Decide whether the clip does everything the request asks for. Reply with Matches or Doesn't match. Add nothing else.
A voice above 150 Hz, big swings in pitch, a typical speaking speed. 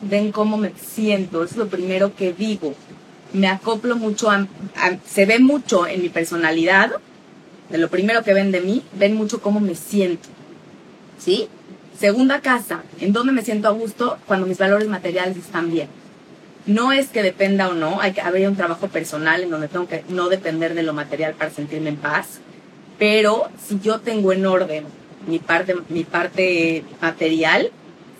Doesn't match